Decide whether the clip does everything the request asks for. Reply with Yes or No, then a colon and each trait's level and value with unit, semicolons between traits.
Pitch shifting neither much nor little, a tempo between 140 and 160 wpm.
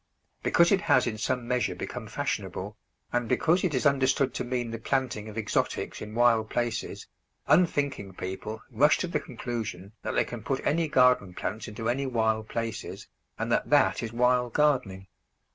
No: average, 3.4 semitones; average, 175 wpm